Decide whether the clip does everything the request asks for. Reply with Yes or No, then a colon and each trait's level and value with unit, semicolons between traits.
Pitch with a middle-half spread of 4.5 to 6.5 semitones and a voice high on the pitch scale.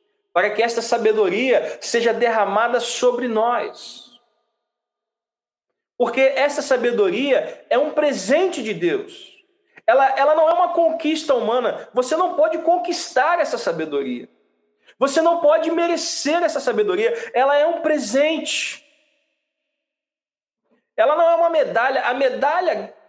Yes: average, 4.8 semitones; very high, 305 Hz